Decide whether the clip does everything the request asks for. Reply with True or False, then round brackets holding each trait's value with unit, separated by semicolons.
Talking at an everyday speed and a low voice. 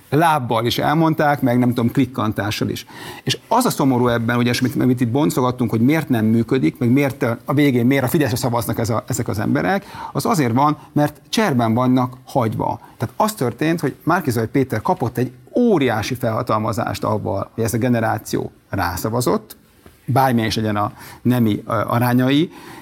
False (170 wpm; 125 Hz)